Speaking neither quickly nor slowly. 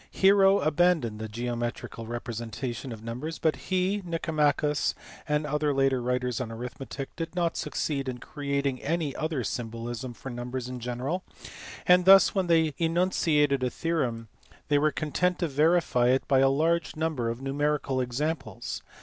Yes: average, 155 wpm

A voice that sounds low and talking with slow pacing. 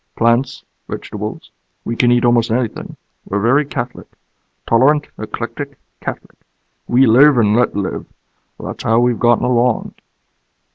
Yes: low, 120 Hz; slow, 130 wpm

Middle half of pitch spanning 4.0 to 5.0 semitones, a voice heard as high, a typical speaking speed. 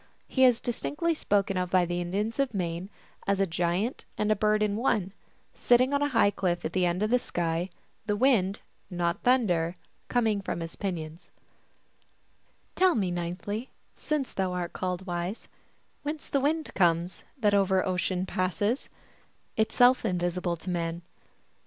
Yes: average, 4.6 semitones; high, 195 Hz; average, 160 wpm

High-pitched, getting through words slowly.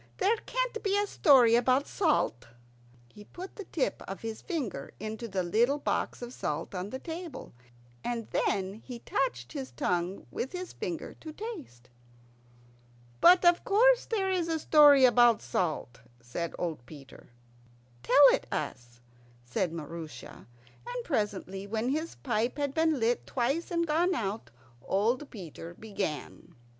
No: high, 240 Hz; average, 150 wpm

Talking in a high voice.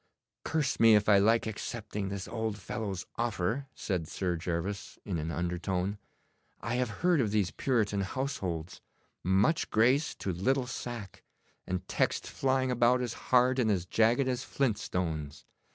No: low, 105 Hz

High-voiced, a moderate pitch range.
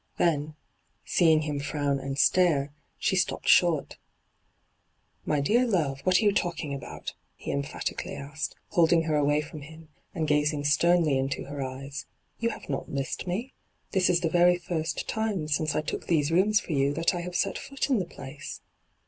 No: medium, 155 Hz; average, 3.7 semitones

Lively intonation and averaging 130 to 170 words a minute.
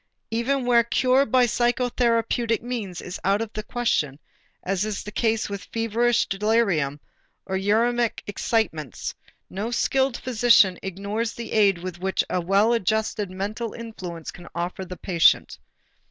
No: average, 3.8 semitones; average, 140 wpm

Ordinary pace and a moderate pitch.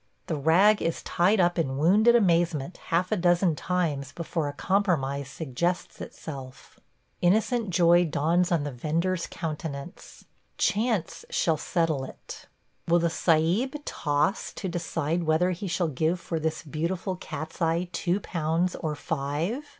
Yes: average, 145 wpm; medium, 170 Hz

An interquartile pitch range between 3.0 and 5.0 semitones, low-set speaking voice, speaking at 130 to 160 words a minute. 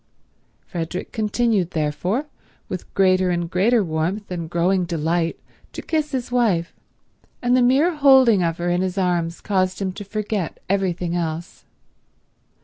No: average, 4.2 semitones; medium, 185 Hz; average, 140 wpm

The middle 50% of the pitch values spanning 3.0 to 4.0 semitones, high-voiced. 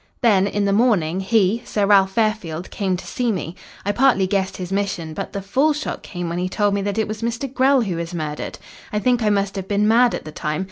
Yes: average, 3.5 semitones; high, 200 Hz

